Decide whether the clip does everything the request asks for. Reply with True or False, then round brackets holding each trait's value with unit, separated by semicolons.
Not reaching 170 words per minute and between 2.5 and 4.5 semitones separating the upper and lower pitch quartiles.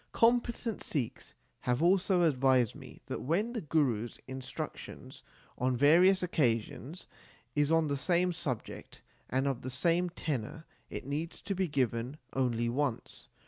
False (140 wpm; 5.6 semitones)